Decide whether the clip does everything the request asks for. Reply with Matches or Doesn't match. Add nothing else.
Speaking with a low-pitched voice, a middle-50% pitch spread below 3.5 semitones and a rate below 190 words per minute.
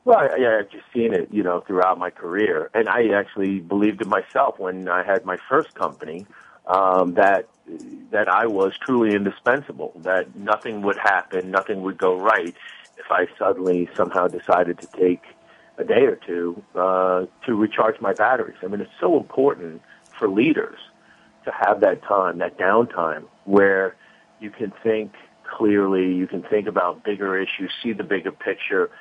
Matches